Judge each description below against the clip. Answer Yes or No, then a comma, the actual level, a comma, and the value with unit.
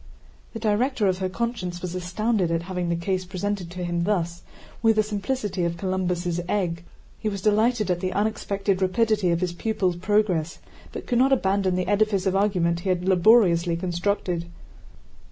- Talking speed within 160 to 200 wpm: Yes, average, 170 wpm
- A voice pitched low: No, medium, 185 Hz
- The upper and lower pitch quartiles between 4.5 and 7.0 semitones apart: No, average, 3.2 semitones